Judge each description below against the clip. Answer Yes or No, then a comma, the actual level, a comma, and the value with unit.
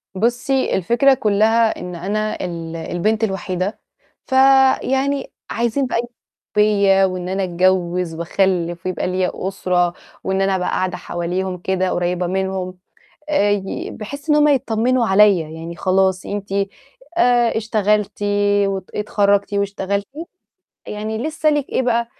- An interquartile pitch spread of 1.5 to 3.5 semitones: No, average, 3.9 semitones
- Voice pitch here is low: No, high, 195 Hz